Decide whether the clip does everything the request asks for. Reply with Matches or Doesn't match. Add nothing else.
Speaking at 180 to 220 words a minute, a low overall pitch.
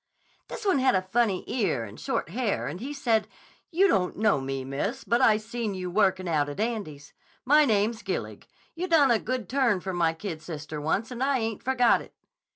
Doesn't match